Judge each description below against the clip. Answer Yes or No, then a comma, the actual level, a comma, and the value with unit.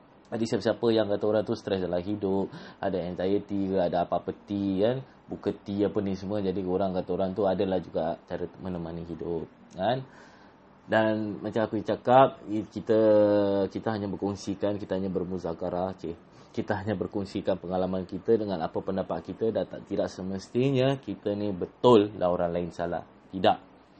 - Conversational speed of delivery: No, fast, 165 wpm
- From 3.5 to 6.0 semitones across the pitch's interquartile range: No, narrow, 2.4 semitones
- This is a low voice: Yes, low, 100 Hz